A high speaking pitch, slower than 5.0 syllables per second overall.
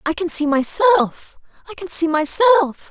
Yes: very high, 340 Hz; 4.8 syllables/s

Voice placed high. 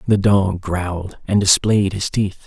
No: very low, 95 Hz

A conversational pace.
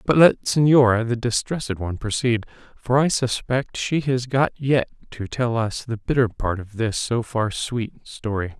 Yes: average, 180 wpm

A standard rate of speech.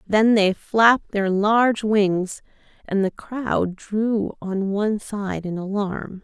Yes: average, 145 wpm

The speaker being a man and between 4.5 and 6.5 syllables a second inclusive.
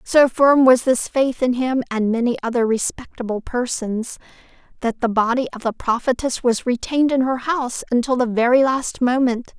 No: female; 5.0 syllables/s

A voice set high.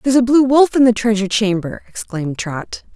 Yes: high, 220 Hz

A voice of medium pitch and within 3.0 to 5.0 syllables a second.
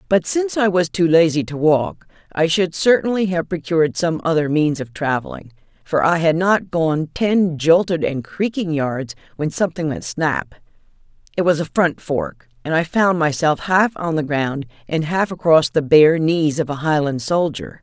Yes: medium, 160 Hz; 4.6 syllables/s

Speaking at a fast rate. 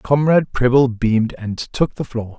No: average, 175 wpm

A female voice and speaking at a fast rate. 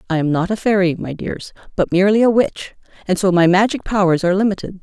Yes: female; fast, 225 wpm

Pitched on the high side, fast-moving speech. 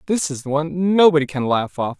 No: medium, 155 Hz; fast, 210 wpm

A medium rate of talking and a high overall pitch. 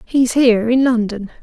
Yes: average, 170 wpm; high, 240 Hz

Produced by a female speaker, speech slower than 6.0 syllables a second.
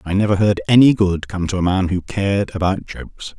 No: male; 5.6 syllables/s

